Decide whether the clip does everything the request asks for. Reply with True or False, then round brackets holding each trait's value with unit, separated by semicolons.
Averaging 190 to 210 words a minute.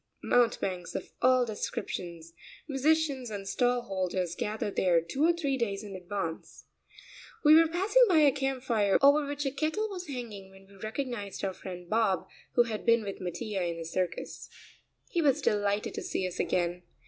False (175 wpm)